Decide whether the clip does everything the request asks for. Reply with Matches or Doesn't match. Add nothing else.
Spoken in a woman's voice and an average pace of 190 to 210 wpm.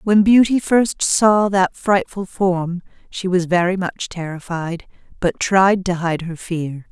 Doesn't match